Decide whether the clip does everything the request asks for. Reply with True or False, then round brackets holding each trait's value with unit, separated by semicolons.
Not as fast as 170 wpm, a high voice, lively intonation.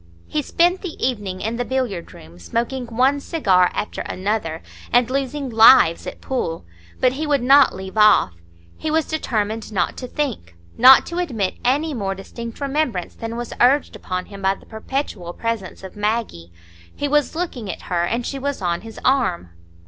False (175 wpm; 230 Hz; 6.1 semitones)